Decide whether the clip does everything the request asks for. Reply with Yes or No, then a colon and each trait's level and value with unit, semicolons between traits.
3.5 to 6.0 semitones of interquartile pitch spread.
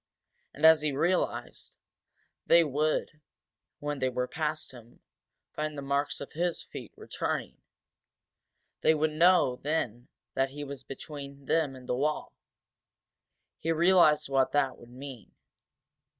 No: average, 2.7 semitones